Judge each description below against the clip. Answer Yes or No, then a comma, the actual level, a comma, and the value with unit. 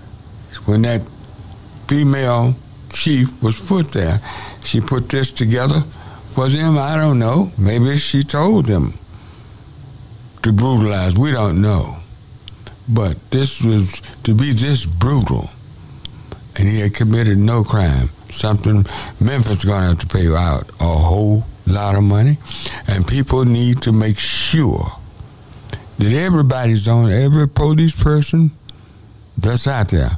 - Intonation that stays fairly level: No, average, 4.3 semitones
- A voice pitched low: Yes, low, 115 Hz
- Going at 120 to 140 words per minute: Yes, slow, 135 wpm